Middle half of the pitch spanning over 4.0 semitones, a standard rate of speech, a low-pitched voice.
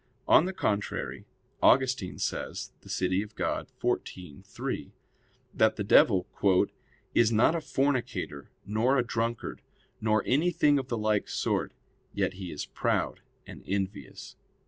No: average, 4.8 semitones; slow, 130 wpm; low, 110 Hz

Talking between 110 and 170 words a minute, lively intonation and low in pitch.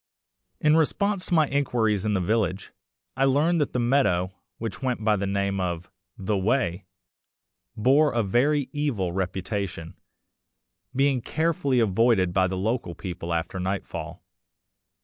Yes: average, 140 wpm; wide, 6.4 semitones; low, 110 Hz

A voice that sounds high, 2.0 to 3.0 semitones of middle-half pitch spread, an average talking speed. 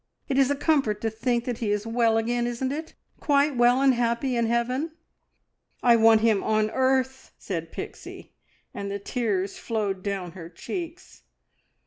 No: high, 235 Hz; average, 3.5 semitones; average, 165 wpm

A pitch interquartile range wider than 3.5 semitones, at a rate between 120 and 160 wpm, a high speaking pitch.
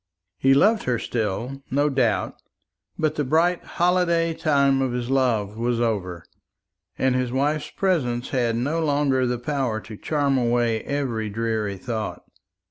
No: average, 4.0 semitones; average, 145 wpm; low, 130 Hz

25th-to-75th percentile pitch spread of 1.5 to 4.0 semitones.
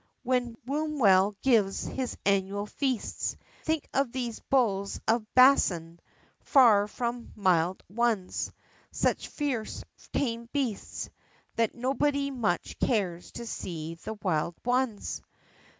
No: average, 4.7 semitones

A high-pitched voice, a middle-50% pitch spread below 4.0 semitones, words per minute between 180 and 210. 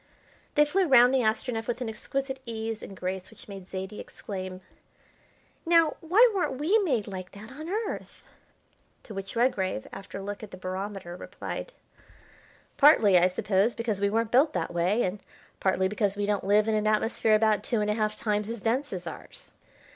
No: high, 215 Hz; average, 4.4 semitones; average, 185 wpm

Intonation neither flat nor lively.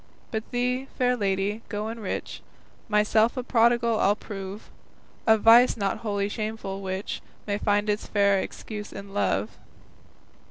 No: narrow, 2.3 semitones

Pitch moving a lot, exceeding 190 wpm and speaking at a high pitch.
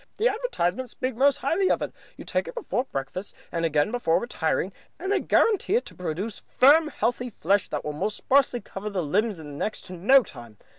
Yes: wide, 8.3 semitones; average, 200 wpm; high, 220 Hz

